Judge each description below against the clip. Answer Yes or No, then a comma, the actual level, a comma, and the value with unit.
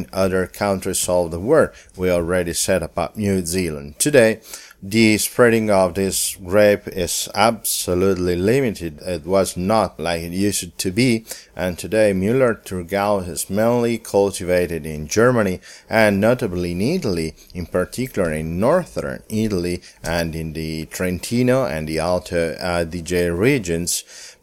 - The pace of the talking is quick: No, average, 140 wpm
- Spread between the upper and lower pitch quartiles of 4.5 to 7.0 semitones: No, average, 3.0 semitones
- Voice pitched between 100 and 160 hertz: No, very low, 90 Hz